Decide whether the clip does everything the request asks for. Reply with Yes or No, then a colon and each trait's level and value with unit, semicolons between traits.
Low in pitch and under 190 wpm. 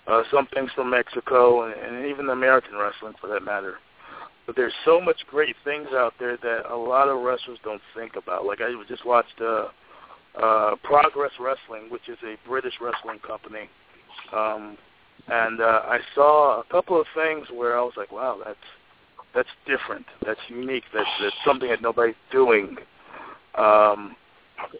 Yes: low, 125 Hz; average, 165 wpm